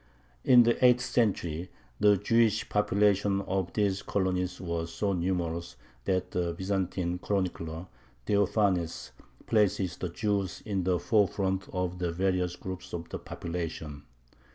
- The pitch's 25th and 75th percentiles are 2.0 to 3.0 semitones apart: Yes, average, 2.7 semitones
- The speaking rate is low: Yes, slow, 130 wpm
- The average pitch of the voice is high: No, very low, 95 Hz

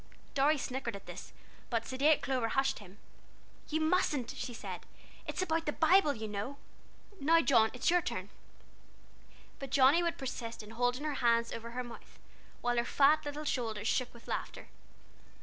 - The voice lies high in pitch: Yes, very high, 260 Hz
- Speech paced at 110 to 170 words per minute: Yes, average, 165 wpm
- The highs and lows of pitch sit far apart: No, average, 4.4 semitones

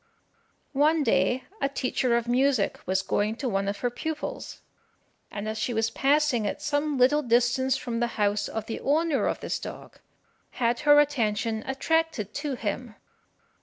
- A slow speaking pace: No, average, 165 wpm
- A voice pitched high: Yes, high, 245 Hz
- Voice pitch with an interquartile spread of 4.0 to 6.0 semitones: Yes, average, 4.7 semitones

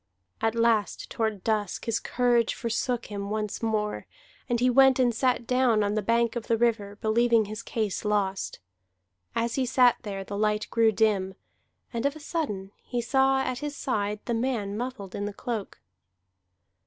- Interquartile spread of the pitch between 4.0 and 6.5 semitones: No, average, 2.7 semitones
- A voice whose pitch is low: No, high, 225 Hz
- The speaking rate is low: No, average, 175 wpm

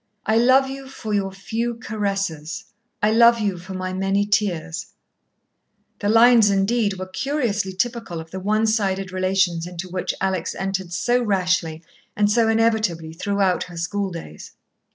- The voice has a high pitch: Yes, high, 195 Hz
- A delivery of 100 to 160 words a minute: Yes, average, 150 wpm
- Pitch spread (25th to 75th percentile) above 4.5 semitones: No, average, 3.2 semitones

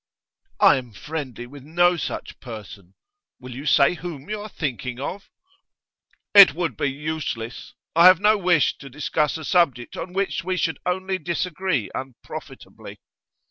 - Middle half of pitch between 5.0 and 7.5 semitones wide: Yes, wide, 5.4 semitones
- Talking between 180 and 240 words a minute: No, average, 150 wpm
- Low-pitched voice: No, medium, 155 Hz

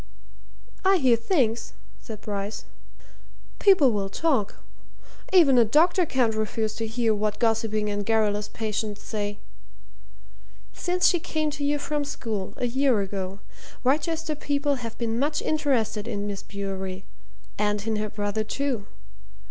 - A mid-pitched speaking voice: No, high, 225 Hz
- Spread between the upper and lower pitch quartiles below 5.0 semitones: No, wide, 5.5 semitones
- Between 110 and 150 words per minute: Yes, average, 140 wpm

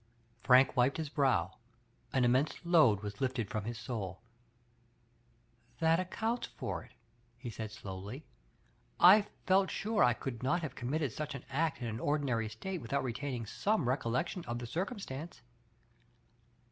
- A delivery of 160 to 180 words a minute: No, average, 150 wpm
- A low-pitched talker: Yes, low, 130 Hz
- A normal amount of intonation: No, wide, 5.7 semitones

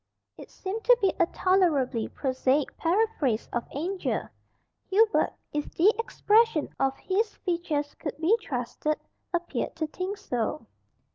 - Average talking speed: No, slow, 130 wpm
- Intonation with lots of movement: Yes, wide, 5.8 semitones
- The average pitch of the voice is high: Yes, very high, 340 Hz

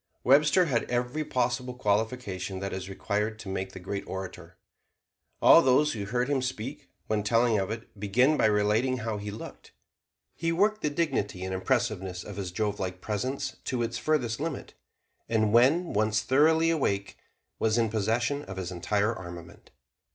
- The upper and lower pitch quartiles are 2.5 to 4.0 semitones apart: No, average, 4.5 semitones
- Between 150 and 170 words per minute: Yes, average, 165 wpm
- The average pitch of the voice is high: No, low, 110 Hz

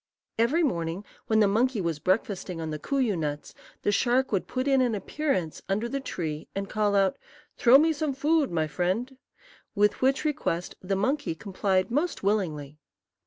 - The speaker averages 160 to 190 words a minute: Yes, average, 170 wpm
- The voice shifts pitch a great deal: Yes, wide, 6.7 semitones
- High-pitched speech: Yes, high, 205 Hz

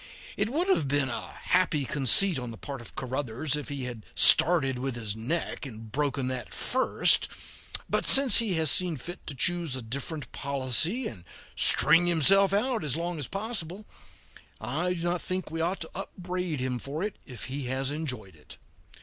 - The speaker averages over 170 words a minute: Yes, average, 185 wpm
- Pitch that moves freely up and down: Yes, wide, 5.7 semitones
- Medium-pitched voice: Yes, medium, 150 Hz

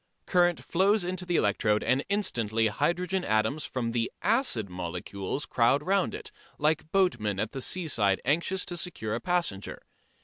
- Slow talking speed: No, average, 150 wpm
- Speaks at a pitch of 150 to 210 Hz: No, medium, 140 Hz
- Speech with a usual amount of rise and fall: No, wide, 8.7 semitones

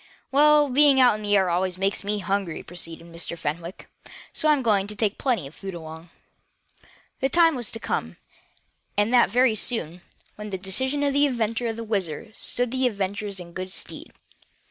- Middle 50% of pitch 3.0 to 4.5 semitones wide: No, average, 5.2 semitones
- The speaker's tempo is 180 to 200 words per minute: Yes, average, 190 wpm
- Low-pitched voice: No, high, 210 Hz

